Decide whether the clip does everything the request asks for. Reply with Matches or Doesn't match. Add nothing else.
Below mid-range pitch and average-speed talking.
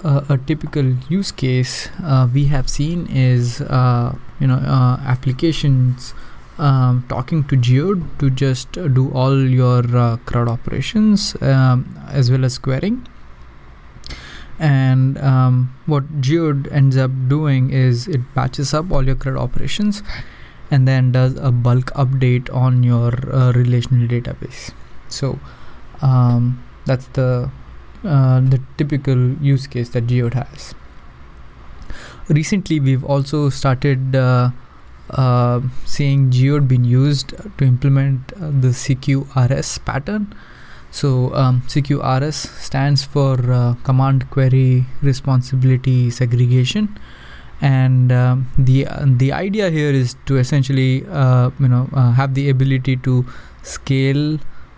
Doesn't match